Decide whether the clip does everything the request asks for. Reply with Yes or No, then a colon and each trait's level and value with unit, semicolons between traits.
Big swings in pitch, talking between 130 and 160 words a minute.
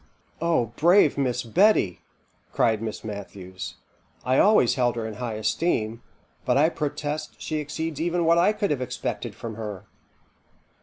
Yes: wide, 6.6 semitones; average, 155 wpm